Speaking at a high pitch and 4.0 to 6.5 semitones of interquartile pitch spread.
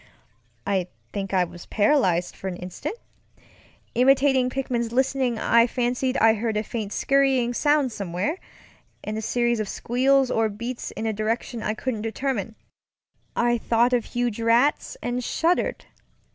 No: high, 235 Hz; average, 3.2 semitones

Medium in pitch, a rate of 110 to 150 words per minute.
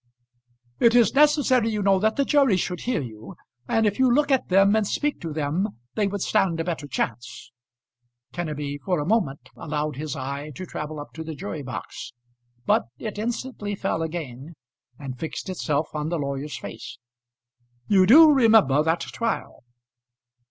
No: medium, 175 Hz; average, 170 wpm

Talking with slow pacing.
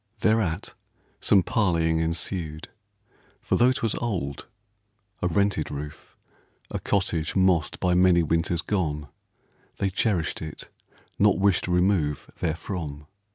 Yes: slow, 120 wpm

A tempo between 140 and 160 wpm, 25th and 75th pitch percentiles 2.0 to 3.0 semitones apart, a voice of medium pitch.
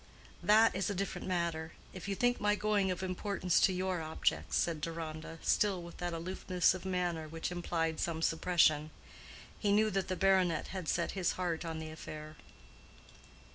No: average, 170 wpm; average, 2.7 semitones; medium, 175 Hz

